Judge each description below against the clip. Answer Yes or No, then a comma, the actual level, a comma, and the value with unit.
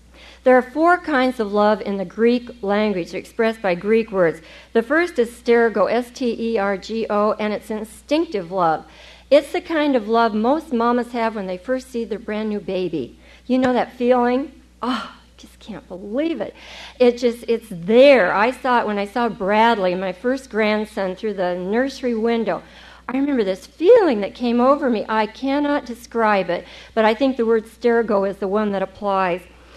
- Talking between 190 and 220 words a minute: No, average, 180 wpm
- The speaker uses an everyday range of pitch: Yes, average, 3.6 semitones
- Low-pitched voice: No, high, 230 Hz